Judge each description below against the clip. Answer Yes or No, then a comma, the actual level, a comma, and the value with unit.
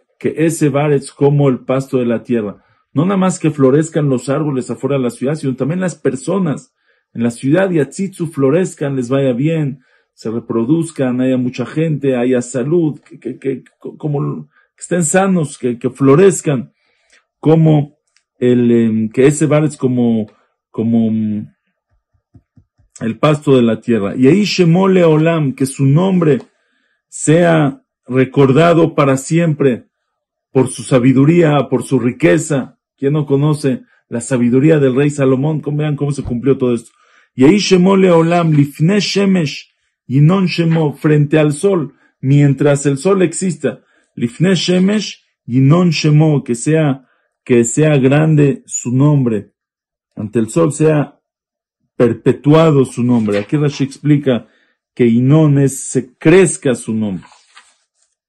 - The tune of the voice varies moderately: Yes, average, 3.7 semitones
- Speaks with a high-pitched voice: No, medium, 140 Hz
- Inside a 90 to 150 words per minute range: Yes, average, 140 wpm